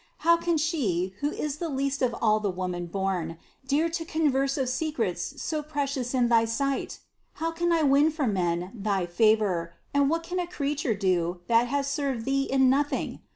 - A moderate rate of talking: Yes, average, 185 wpm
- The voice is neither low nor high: No, very high, 265 Hz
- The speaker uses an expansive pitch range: Yes, wide, 7.0 semitones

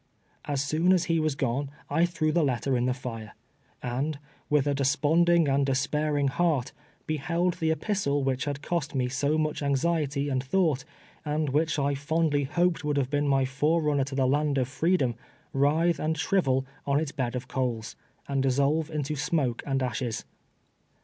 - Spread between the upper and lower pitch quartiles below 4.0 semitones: Yes, average, 2.8 semitones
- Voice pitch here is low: No, medium, 145 Hz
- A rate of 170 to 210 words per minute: Yes, average, 175 wpm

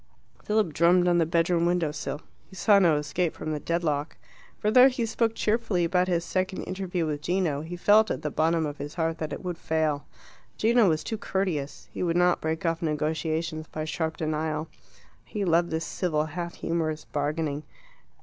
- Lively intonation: No, average, 2.7 semitones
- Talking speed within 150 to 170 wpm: No, average, 190 wpm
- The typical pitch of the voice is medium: Yes, medium, 165 Hz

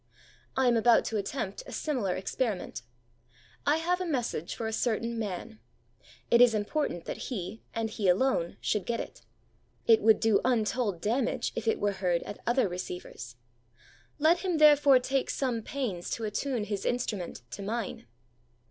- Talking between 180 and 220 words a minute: No, average, 165 wpm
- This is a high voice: Yes, high, 225 Hz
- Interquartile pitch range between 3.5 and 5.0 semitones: Yes, average, 4.4 semitones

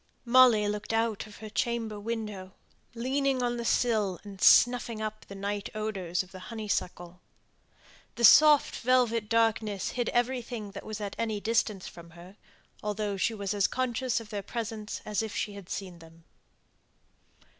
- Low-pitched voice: No, high, 215 Hz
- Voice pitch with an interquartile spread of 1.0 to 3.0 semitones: Yes, average, 2.7 semitones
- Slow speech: No, average, 160 wpm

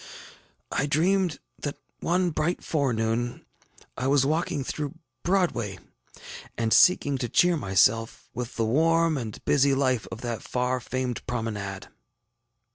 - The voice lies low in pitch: Yes, low, 130 Hz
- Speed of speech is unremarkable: No, slow, 125 wpm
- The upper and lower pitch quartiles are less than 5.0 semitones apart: No, wide, 5.5 semitones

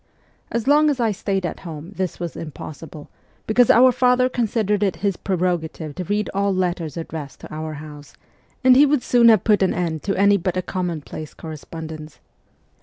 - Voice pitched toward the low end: No, medium, 185 Hz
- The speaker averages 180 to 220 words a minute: Yes, average, 185 wpm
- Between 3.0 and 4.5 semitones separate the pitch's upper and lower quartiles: No, average, 5.3 semitones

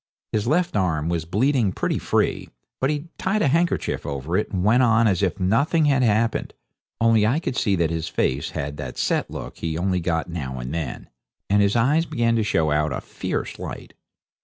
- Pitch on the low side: Yes, low, 100 Hz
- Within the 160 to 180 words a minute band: No, fast, 205 wpm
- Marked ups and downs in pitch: Yes, wide, 7.3 semitones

